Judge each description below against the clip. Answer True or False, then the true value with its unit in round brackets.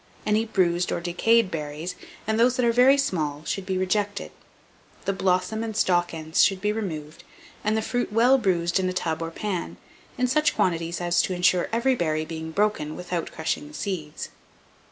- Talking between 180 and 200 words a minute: True (185 wpm)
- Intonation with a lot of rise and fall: False (4.7 semitones)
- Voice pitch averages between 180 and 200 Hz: True (185 Hz)